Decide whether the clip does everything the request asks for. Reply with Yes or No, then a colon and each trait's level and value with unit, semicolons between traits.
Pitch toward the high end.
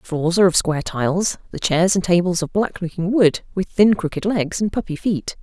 No: medium, 180 Hz